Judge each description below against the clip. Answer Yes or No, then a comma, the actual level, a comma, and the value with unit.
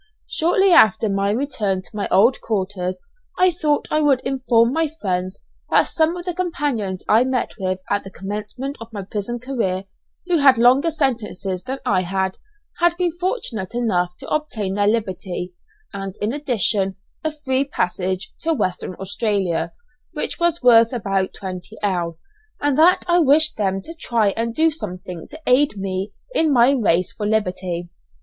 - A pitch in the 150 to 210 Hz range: No, high, 220 Hz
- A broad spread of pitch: Yes, wide, 7.0 semitones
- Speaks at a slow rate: No, average, 165 wpm